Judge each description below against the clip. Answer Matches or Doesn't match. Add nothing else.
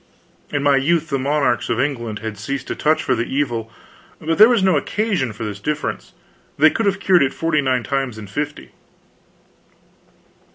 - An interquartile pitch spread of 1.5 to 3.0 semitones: Doesn't match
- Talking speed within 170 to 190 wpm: Matches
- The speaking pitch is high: Doesn't match